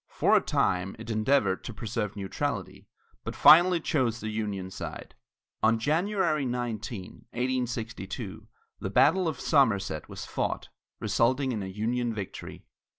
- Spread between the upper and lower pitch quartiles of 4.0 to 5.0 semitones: Yes, average, 4.3 semitones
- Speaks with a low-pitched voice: Yes, low, 115 Hz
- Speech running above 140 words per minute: No, slow, 135 wpm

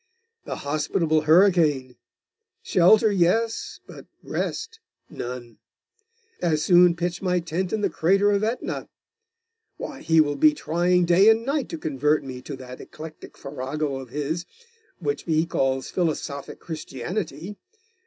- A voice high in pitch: No, medium, 165 Hz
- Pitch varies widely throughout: No, average, 4.6 semitones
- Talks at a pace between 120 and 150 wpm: Yes, slow, 135 wpm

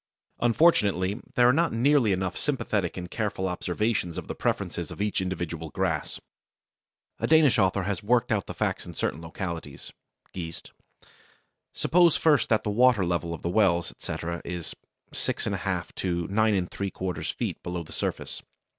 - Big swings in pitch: No, average, 4.7 semitones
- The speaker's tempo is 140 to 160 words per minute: Yes, average, 155 wpm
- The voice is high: No, very low, 95 Hz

